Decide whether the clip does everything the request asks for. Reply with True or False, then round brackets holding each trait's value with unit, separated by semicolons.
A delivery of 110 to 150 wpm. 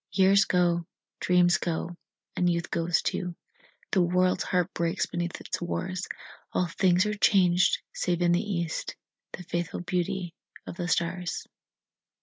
True (140 wpm)